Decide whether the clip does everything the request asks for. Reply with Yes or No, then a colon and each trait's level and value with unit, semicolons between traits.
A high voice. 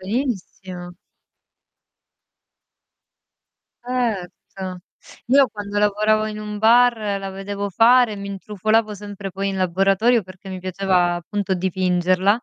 Yes: high, 200 Hz